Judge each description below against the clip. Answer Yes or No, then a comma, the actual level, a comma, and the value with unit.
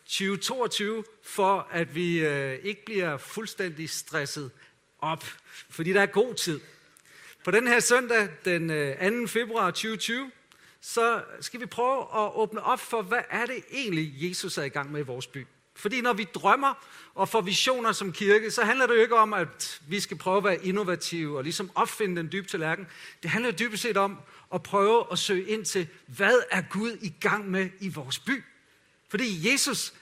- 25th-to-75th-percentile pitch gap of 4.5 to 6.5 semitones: Yes, average, 4.8 semitones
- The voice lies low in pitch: No, high, 200 Hz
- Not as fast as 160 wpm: No, average, 185 wpm